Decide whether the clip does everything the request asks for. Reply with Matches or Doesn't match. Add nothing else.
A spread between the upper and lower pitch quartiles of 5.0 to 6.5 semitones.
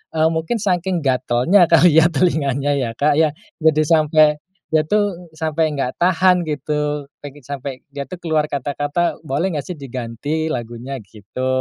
Doesn't match